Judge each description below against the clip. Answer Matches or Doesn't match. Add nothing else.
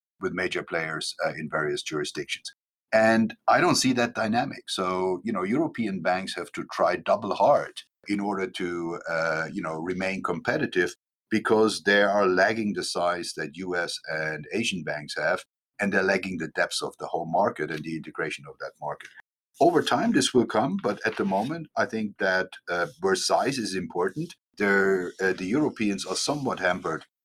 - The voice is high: Doesn't match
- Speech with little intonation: Doesn't match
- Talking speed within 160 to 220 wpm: Matches